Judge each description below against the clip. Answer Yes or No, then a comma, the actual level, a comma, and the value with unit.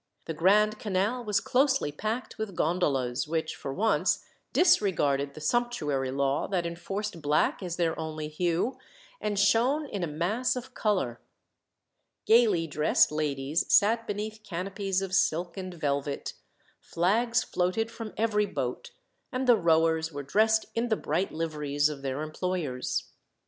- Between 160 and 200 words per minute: No, average, 145 wpm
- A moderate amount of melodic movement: No, wide, 6.0 semitones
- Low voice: No, medium, 180 Hz